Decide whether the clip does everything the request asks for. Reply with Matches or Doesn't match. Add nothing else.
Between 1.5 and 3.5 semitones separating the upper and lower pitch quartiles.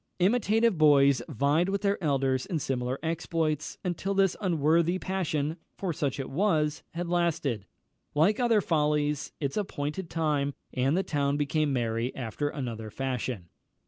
Doesn't match